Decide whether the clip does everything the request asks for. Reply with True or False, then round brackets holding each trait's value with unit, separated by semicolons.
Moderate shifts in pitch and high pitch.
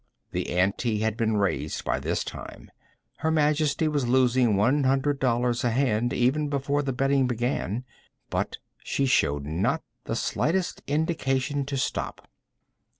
False (3.6 semitones; 130 Hz)